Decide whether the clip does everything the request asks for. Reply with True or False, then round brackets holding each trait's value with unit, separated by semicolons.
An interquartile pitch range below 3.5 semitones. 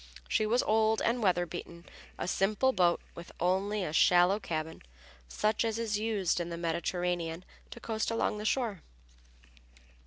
False (4.0 semitones)